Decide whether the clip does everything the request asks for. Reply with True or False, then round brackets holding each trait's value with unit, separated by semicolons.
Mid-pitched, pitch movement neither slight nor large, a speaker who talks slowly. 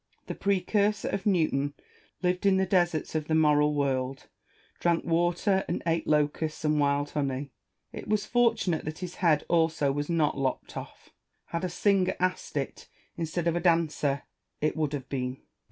False (160 Hz; 3.6 semitones; 175 wpm)